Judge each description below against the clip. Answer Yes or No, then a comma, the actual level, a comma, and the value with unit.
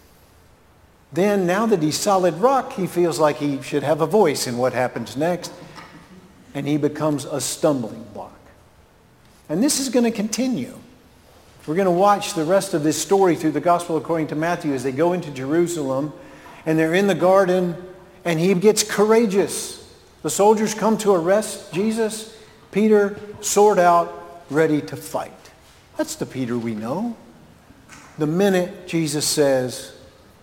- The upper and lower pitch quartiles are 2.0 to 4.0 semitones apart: No, average, 5.0 semitones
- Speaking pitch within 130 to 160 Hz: No, medium, 175 Hz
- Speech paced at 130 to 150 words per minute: No, average, 160 wpm